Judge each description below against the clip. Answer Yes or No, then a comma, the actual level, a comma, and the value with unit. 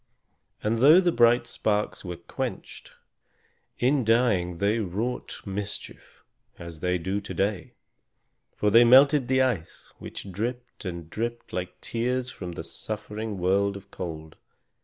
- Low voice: Yes, low, 105 Hz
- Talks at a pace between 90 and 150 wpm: Yes, average, 140 wpm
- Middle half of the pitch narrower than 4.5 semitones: No, average, 4.8 semitones